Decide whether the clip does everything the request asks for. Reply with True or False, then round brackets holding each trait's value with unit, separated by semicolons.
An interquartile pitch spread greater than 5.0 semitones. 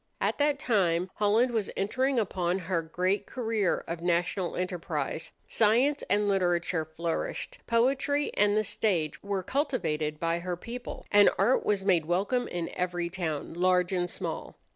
False (4.3 semitones)